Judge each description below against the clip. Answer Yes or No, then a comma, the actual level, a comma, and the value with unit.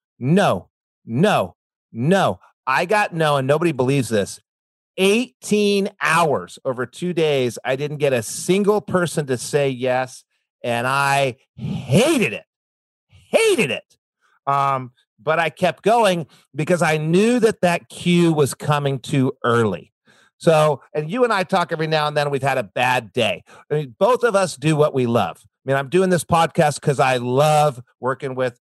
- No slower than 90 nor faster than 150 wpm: No, average, 170 wpm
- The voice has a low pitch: No, medium, 150 Hz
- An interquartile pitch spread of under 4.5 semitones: No, average, 5.0 semitones